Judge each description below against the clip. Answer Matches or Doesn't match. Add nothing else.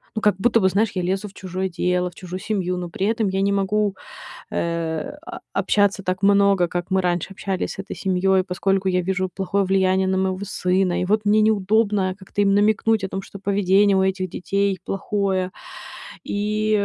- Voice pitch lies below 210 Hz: Matches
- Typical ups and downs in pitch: Doesn't match